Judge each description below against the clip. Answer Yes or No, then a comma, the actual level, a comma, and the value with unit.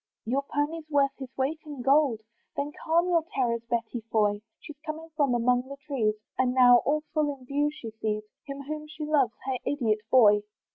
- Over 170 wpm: Yes, average, 190 wpm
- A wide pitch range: No, average, 3.9 semitones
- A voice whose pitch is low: No, very high, 275 Hz